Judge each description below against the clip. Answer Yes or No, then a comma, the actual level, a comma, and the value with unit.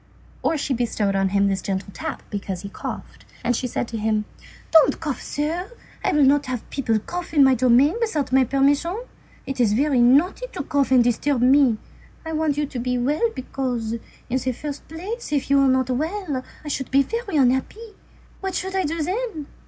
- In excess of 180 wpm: Yes, average, 200 wpm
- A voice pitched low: No, very high, 275 Hz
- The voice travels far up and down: No, average, 4.3 semitones